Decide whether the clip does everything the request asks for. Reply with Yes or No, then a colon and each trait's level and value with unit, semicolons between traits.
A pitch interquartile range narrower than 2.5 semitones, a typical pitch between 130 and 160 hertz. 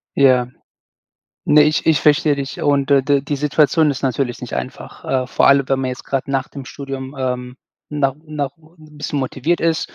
Yes: narrow, 2.1 semitones; medium, 140 Hz